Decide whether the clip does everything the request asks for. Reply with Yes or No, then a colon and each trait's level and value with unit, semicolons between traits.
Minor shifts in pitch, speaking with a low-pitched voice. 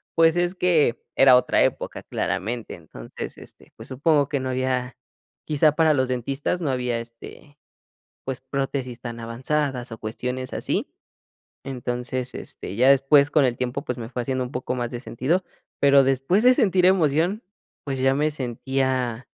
No: average, 3.0 semitones; low, 130 Hz